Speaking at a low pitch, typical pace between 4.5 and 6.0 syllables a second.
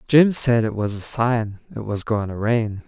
No: low, 115 Hz; 4.3 syllables/s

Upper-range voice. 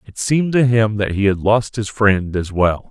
No: low, 105 Hz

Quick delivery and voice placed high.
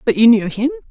Yes: fast, 265 wpm; high, 235 Hz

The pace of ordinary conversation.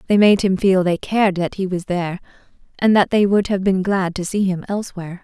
No: fast, 240 wpm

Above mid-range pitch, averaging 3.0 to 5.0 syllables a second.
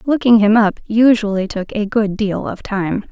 Yes: high, 210 Hz; 4.5 syllables/s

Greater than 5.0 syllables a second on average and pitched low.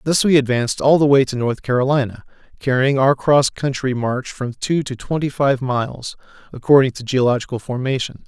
Yes: 5.4 syllables/s; low, 130 Hz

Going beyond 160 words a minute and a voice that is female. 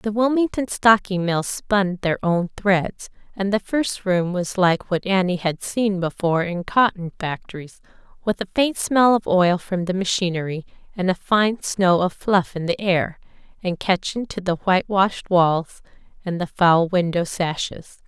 Yes: average, 175 wpm; female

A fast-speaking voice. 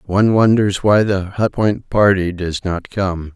No: average, 180 wpm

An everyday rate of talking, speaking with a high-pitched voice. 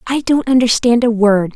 Yes: average, 195 wpm; high, 235 Hz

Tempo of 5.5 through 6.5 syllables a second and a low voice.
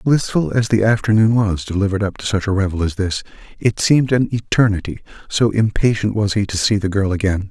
Yes: 5.9 syllables/s; low, 105 Hz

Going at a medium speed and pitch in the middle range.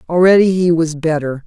Yes: average, 165 wpm; medium, 165 Hz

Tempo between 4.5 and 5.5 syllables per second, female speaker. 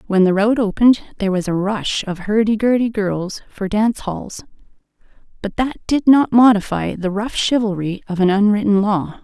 Yes: 5.0 syllables/s; female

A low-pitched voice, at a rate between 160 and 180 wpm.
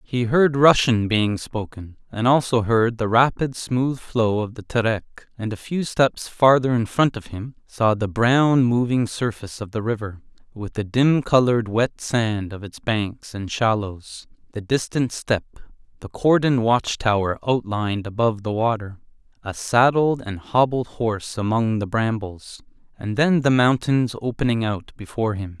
Yes: low, 115 Hz; average, 165 wpm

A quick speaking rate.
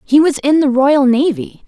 Yes: fast, 215 wpm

